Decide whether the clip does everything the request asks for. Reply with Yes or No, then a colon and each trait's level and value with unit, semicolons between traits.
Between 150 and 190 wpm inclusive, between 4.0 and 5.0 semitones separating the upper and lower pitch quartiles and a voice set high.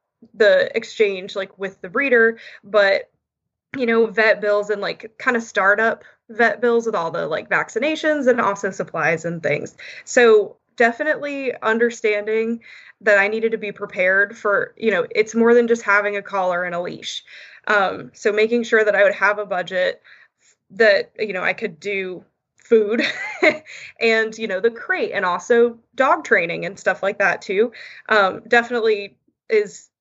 No: average, 170 wpm; average, 3.6 semitones; high, 225 Hz